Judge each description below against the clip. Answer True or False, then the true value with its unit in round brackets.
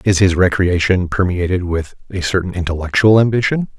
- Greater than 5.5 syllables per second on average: False (5.4 syllables/s)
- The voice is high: False (95 Hz)